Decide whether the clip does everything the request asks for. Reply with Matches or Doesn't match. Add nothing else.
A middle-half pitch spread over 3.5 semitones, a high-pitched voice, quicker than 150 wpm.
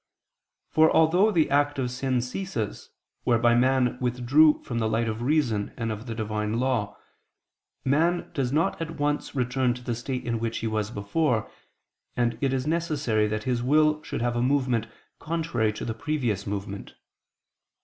Doesn't match